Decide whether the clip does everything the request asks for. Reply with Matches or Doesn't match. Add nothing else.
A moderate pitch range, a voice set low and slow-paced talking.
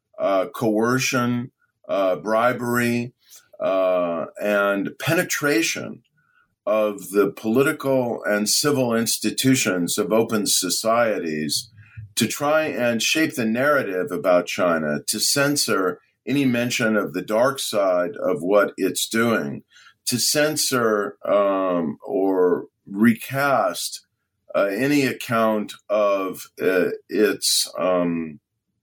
Matches